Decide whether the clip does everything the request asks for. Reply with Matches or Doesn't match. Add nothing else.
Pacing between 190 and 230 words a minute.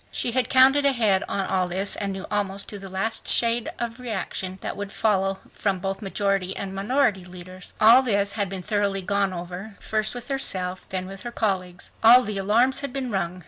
Matches